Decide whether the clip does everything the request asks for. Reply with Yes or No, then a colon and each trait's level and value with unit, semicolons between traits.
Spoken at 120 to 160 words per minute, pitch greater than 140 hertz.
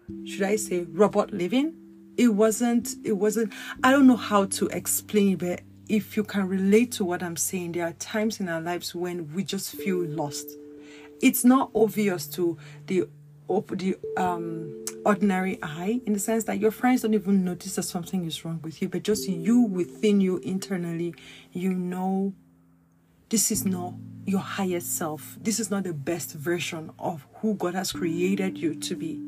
No: average, 180 wpm; medium, 185 Hz